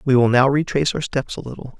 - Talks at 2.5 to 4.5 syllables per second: No, 6.5 syllables/s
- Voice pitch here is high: No, low, 135 Hz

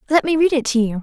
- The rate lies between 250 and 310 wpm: No, fast, 350 wpm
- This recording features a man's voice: No, female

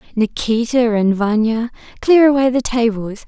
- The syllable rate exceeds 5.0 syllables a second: No, 4.6 syllables/s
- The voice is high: Yes, high, 235 Hz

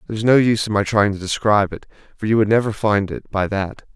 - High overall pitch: No, low, 105 Hz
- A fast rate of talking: Yes, fast, 245 wpm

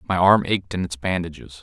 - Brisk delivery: Yes, fast, 220 wpm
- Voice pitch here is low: Yes, very low, 90 Hz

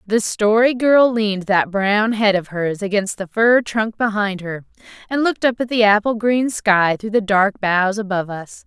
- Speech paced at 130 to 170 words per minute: No, average, 200 wpm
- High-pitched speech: Yes, high, 210 Hz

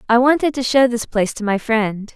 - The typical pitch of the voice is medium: No, high, 235 Hz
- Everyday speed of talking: No, fast, 250 wpm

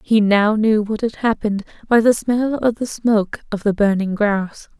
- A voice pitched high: Yes, high, 215 Hz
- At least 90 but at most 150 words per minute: No, average, 200 wpm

